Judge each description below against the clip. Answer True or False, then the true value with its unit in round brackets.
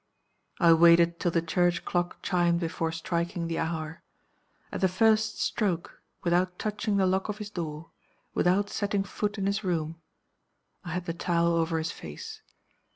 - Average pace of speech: True (160 wpm)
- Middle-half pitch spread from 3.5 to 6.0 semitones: False (3.0 semitones)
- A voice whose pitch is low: False (175 Hz)